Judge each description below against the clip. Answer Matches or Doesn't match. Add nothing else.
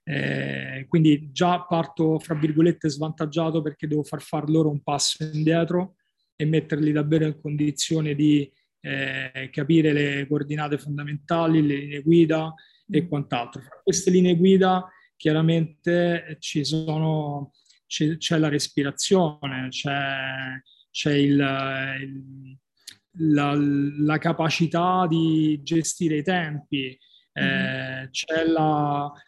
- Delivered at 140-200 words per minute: Doesn't match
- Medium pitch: Matches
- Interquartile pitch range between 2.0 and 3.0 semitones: Matches